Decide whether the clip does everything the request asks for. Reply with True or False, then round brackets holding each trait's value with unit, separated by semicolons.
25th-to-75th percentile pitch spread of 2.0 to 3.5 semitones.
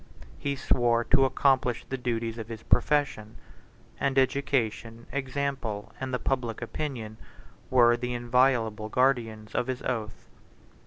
True (2.8 semitones)